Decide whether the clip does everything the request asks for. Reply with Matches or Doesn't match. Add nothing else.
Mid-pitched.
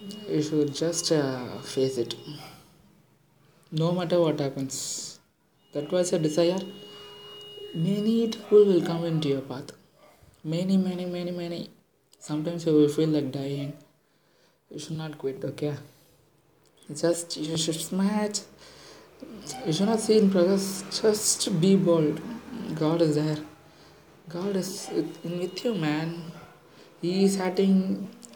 Matches